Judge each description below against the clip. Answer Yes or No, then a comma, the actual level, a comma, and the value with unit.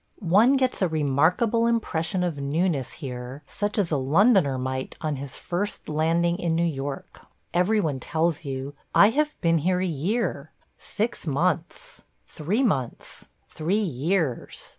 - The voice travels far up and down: Yes, wide, 6.0 semitones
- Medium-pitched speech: Yes, medium, 165 Hz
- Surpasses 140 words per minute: Yes, average, 160 wpm